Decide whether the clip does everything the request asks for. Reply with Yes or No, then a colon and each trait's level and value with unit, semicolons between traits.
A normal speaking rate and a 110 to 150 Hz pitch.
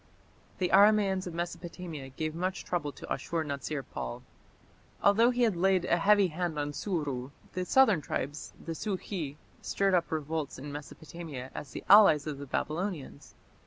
No: average, 160 wpm; medium, 170 Hz